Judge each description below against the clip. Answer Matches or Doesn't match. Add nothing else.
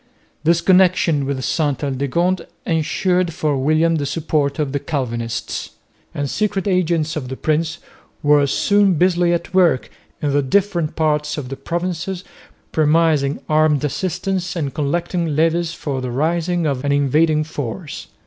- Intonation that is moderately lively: Matches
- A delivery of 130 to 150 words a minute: Matches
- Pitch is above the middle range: Doesn't match